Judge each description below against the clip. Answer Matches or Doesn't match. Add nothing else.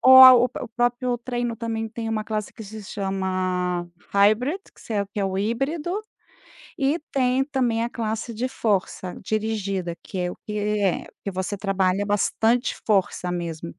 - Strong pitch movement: Doesn't match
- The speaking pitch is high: Matches